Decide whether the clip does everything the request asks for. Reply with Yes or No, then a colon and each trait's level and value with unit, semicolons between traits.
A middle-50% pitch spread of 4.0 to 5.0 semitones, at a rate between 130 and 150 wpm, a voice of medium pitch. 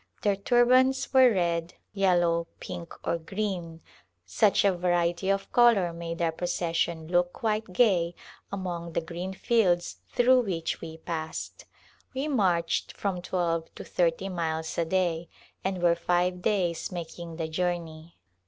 No: average, 2.7 semitones; average, 145 wpm; medium, 175 Hz